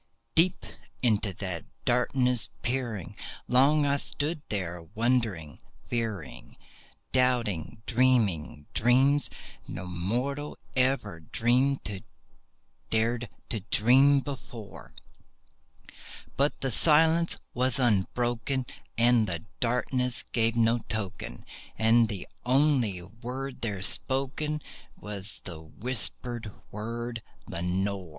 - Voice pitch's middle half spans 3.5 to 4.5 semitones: Yes, average, 4.2 semitones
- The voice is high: No, low, 120 Hz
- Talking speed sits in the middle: No, slow, 90 wpm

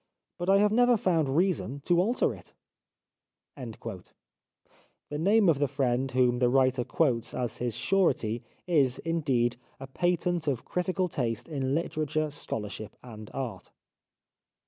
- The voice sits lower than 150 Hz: Yes, medium, 140 Hz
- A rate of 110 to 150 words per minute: Yes, slow, 135 wpm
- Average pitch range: No, wide, 6.2 semitones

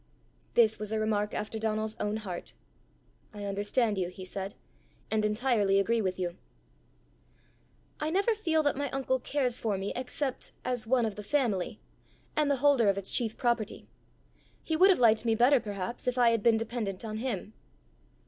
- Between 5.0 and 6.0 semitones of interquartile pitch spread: No, average, 3.7 semitones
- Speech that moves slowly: No, average, 175 wpm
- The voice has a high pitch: Yes, high, 220 Hz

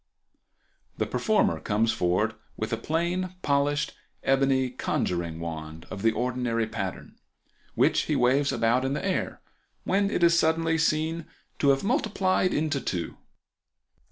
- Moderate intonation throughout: No, wide, 6.5 semitones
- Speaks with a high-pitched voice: No, low, 135 Hz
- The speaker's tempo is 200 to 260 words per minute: No, slow, 135 wpm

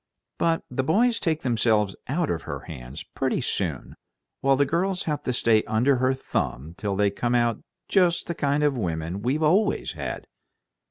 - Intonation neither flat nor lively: No, wide, 7.0 semitones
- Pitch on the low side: Yes, low, 130 Hz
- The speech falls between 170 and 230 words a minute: Yes, average, 175 wpm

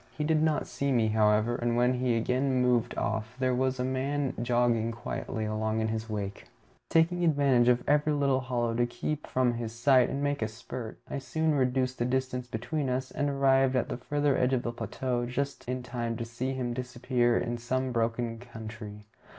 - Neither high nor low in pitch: No, low, 125 Hz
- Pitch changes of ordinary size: No, narrow, 2.2 semitones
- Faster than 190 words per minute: Yes, average, 200 wpm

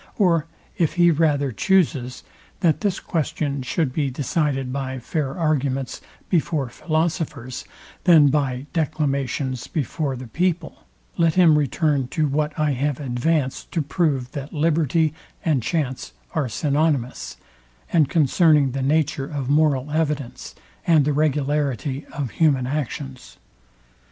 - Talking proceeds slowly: Yes, slow, 125 wpm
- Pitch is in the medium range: Yes, medium, 145 Hz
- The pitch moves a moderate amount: Yes, average, 3.0 semitones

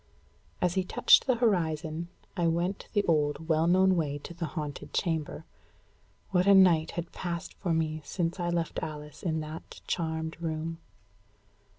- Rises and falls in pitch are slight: Yes, narrow, 2.1 semitones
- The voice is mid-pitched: Yes, medium, 165 Hz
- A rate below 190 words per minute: Yes, average, 160 wpm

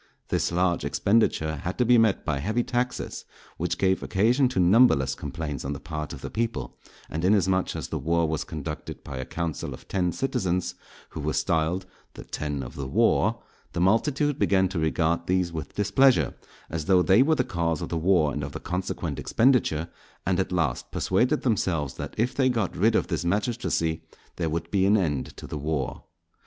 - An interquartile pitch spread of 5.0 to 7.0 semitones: Yes, wide, 5.4 semitones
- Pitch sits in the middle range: No, very low, 90 Hz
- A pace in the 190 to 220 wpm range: Yes, average, 195 wpm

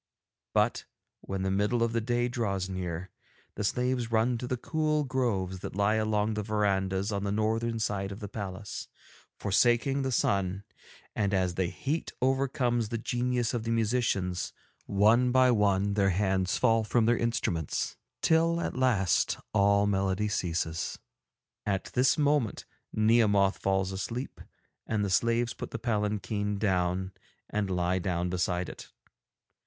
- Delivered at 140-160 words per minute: Yes, average, 150 wpm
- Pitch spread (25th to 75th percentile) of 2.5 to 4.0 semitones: Yes, average, 3.7 semitones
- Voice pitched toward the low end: Yes, low, 105 Hz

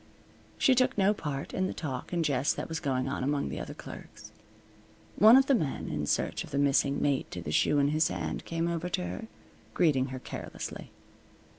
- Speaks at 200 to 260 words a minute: Yes, fast, 205 wpm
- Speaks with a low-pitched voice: No, medium, 145 Hz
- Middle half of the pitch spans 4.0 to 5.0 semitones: Yes, average, 4.3 semitones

